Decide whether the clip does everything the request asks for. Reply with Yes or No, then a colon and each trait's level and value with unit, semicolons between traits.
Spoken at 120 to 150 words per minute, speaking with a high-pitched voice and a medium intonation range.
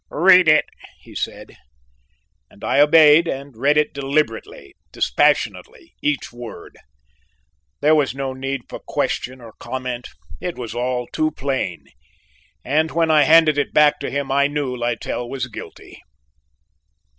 No: average, 140 wpm; medium, 140 Hz; average, 3.2 semitones